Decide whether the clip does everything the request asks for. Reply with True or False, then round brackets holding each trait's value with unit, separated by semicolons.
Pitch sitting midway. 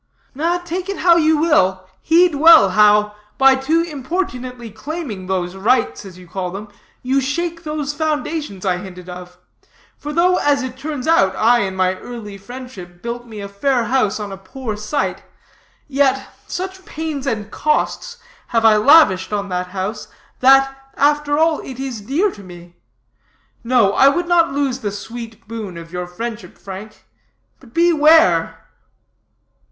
False (250 Hz)